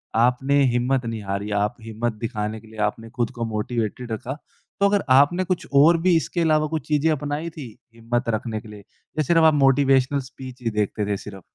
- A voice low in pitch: Yes, low, 125 Hz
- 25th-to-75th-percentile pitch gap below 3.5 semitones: No, average, 5.2 semitones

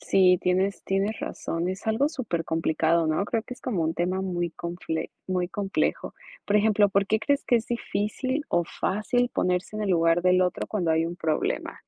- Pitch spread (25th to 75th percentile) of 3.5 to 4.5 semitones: Yes, average, 3.8 semitones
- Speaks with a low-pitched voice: No, medium, 185 Hz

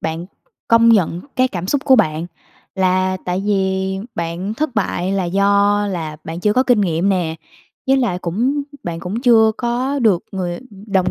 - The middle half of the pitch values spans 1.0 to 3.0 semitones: No, average, 4.2 semitones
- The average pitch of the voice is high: Yes, high, 195 Hz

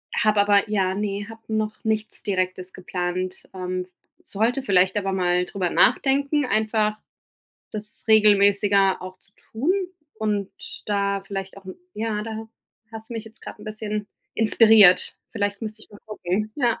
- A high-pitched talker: Yes, high, 210 Hz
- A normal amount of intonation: No, narrow, 2.2 semitones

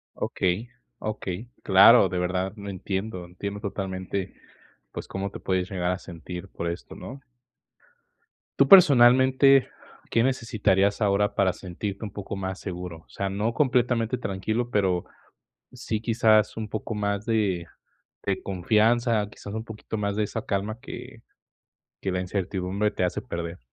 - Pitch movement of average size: Yes, average, 3.1 semitones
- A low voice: Yes, low, 100 Hz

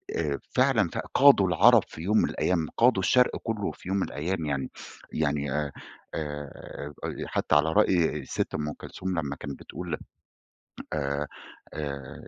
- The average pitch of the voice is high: No, very low, 80 Hz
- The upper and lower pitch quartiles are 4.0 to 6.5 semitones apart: Yes, average, 4.6 semitones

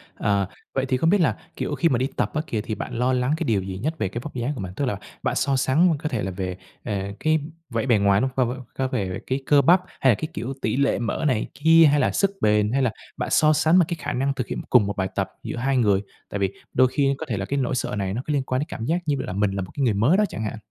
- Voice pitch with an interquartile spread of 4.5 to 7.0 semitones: Yes, wide, 5.4 semitones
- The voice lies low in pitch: Yes, low, 130 Hz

